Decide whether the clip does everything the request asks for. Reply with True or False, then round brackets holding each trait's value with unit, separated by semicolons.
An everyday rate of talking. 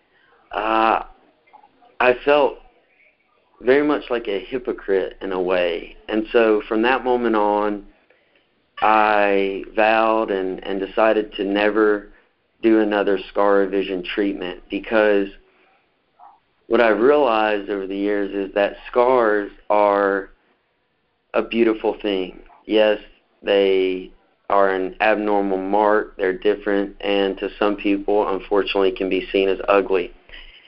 False (120 wpm)